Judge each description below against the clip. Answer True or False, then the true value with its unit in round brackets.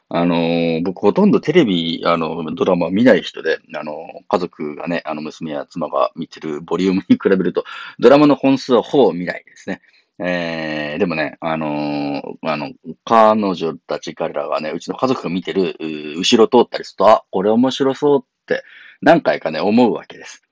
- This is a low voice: True (85 Hz)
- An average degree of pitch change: False (7.0 semitones)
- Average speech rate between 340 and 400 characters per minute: True (345 characters per minute)